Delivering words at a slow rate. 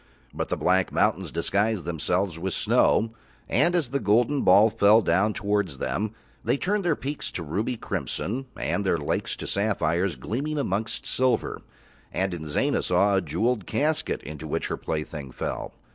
No: average, 160 wpm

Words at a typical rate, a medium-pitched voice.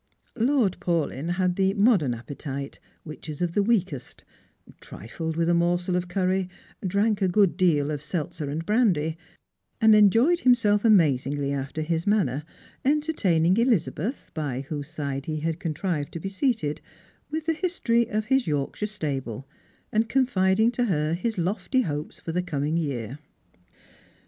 Yes: average, 155 wpm; medium, 175 Hz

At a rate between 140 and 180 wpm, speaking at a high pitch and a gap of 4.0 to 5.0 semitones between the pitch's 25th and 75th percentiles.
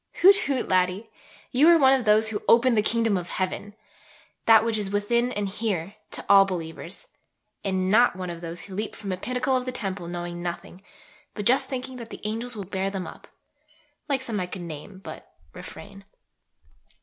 No: average, 195 wpm; high, 205 Hz; average, 4.5 semitones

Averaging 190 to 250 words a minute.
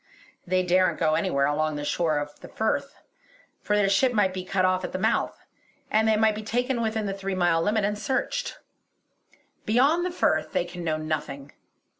Yes: average, 195 wpm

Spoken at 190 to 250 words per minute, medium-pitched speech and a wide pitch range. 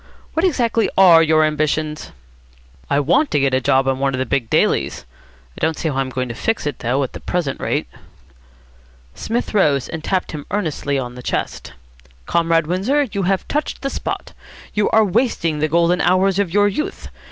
Yes: average, 195 wpm; medium, 165 Hz; wide, 6.3 semitones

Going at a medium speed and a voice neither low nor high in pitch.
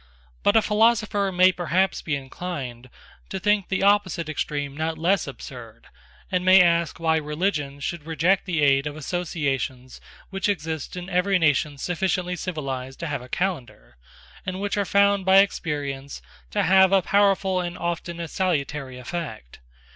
Yes: average, 155 wpm; medium, 170 Hz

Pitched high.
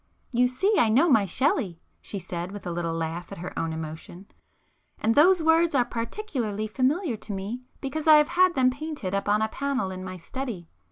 Yes: high, 230 Hz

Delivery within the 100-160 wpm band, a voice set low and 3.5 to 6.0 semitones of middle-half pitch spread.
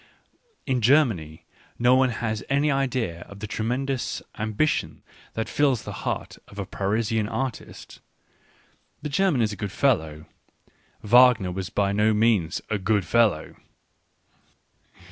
Yes: slow, 135 wpm; low, 110 Hz; average, 4.3 semitones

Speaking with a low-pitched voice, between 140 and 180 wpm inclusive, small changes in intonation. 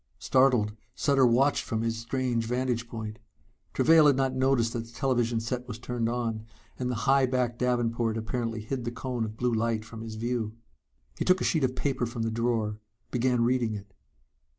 No: low, 120 Hz; average, 190 wpm; narrow, 2.1 semitones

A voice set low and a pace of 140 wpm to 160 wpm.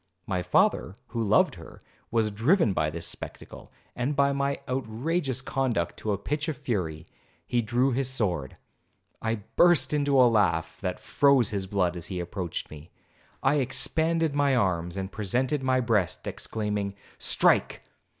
Yes: low, 115 Hz; average, 150 wpm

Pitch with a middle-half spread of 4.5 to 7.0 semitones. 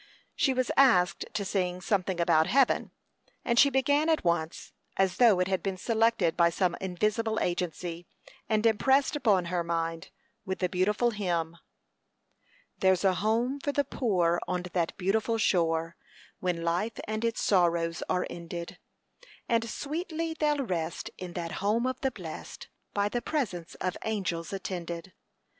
Yes: average, 5.0 semitones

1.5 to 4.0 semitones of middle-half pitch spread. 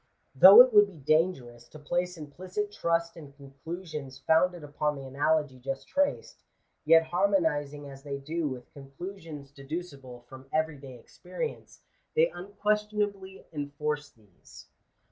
No: average, 4.8 semitones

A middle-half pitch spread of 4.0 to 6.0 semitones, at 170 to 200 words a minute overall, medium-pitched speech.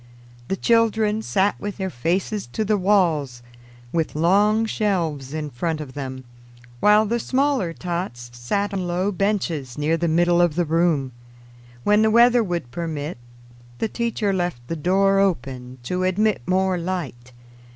No: average, 5.2 semitones; average, 150 wpm; medium, 180 Hz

